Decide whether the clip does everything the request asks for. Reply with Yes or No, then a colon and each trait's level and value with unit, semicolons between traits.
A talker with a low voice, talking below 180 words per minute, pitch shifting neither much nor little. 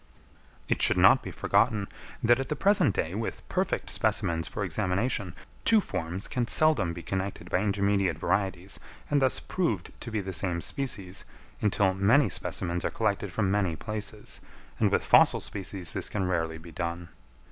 Yes: low, 100 Hz; average, 170 wpm; average, 3.9 semitones